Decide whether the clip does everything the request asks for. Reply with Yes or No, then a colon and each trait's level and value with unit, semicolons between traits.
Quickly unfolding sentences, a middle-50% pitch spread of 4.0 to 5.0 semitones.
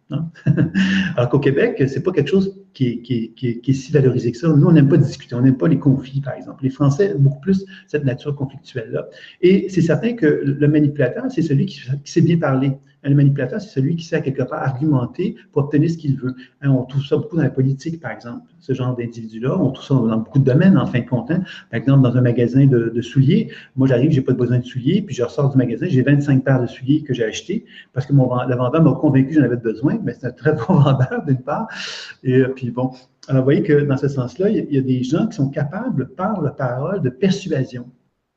No: fast, 265 wpm; average, 3.5 semitones